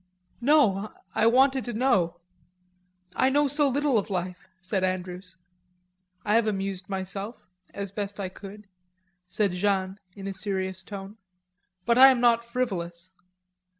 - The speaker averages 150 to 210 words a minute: No, average, 140 wpm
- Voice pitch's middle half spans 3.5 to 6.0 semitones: Yes, average, 4.0 semitones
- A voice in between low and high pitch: No, high, 200 Hz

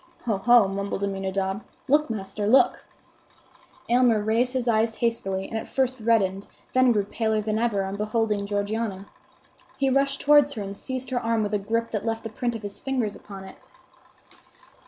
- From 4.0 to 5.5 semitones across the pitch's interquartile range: No, average, 3.2 semitones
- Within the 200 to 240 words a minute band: No, average, 175 wpm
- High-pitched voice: Yes, high, 220 Hz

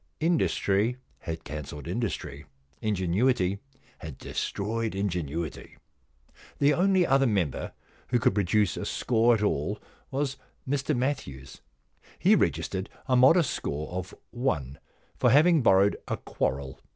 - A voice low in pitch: Yes, low, 105 Hz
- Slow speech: Yes, slow, 125 wpm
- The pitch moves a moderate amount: No, wide, 7.5 semitones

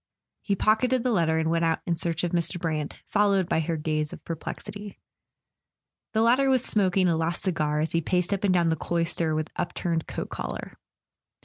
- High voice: No, medium, 170 Hz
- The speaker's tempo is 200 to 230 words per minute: Yes, fast, 205 wpm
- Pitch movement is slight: No, average, 3.6 semitones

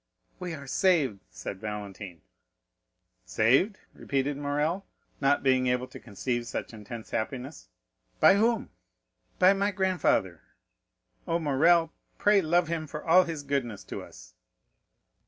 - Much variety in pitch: Yes, wide, 6.6 semitones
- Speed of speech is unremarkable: No, slow, 125 wpm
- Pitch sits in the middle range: Yes, medium, 145 Hz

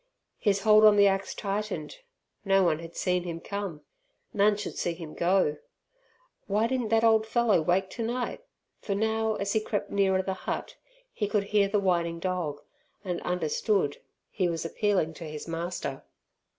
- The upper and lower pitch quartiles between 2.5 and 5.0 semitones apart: Yes, average, 3.7 semitones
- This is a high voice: Yes, high, 195 Hz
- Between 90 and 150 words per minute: No, average, 165 wpm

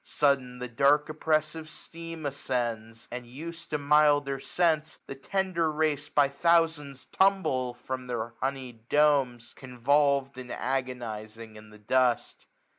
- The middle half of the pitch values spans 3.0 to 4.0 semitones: Yes, average, 3.6 semitones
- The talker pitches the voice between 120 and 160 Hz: Yes, medium, 140 Hz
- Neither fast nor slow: No, slow, 125 wpm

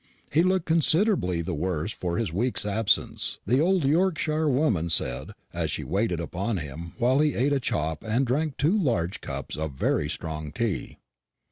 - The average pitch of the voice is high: No, low, 115 Hz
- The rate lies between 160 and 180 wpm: Yes, average, 170 wpm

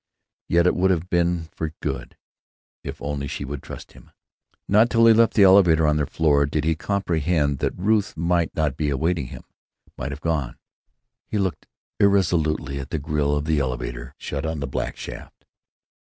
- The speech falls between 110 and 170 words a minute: No, average, 185 wpm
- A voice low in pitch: Yes, very low, 80 Hz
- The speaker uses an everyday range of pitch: Yes, average, 3.8 semitones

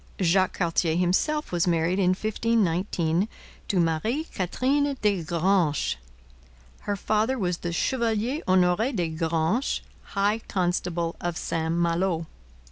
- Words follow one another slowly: Yes, slow, 120 wpm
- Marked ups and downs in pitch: No, average, 4.2 semitones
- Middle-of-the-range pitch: Yes, medium, 180 Hz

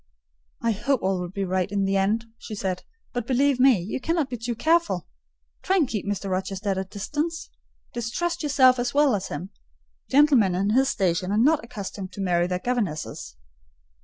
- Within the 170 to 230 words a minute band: Yes, average, 190 wpm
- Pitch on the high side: Yes, high, 215 Hz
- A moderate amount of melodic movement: No, wide, 5.9 semitones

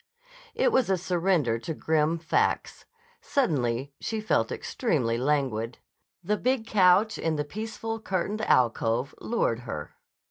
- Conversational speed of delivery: No, slow, 130 wpm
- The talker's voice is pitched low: No, medium, 165 Hz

